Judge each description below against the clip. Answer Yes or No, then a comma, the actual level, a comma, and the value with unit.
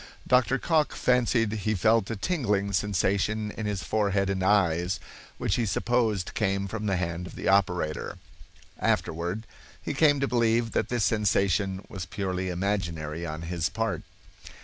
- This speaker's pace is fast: No, average, 150 wpm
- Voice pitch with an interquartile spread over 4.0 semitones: No, average, 3.5 semitones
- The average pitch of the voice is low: Yes, low, 100 Hz